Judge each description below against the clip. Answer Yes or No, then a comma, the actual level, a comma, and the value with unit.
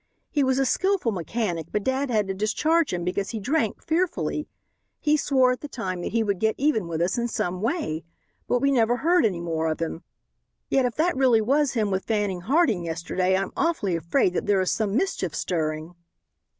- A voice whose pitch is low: No, high, 220 Hz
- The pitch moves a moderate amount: No, wide, 7.0 semitones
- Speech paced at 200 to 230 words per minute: Yes, fast, 205 wpm